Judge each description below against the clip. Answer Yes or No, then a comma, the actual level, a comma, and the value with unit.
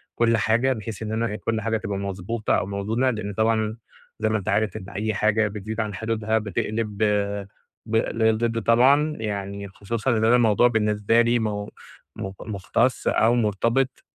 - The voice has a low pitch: Yes, low, 110 Hz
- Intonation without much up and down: Yes, narrow, 1.8 semitones